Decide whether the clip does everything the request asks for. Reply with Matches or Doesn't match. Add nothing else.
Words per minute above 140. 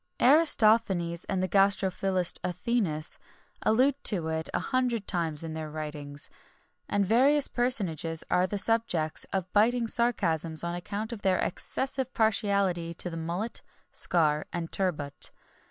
Doesn't match